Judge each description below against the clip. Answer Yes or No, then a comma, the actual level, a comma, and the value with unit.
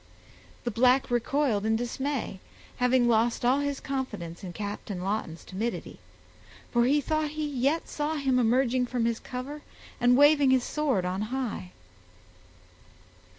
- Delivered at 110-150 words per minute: Yes, average, 140 wpm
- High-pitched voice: Yes, very high, 250 Hz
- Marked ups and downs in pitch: No, average, 3.8 semitones